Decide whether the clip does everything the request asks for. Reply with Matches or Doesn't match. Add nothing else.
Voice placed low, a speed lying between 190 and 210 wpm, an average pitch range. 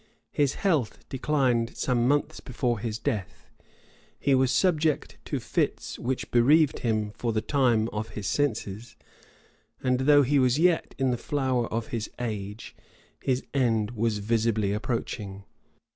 Doesn't match